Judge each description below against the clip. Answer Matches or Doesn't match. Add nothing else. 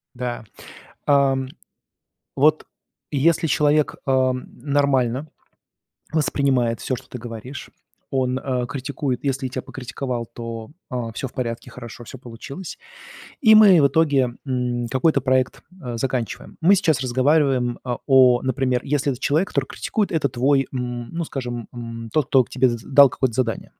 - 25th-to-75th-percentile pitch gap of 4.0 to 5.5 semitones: Doesn't match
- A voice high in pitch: Doesn't match